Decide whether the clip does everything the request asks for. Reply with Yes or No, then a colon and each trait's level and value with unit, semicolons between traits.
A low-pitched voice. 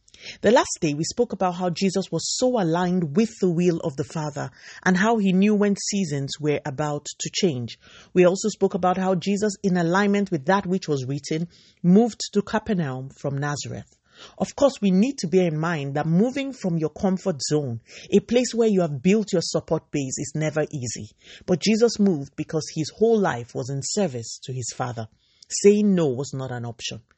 No: medium, 175 Hz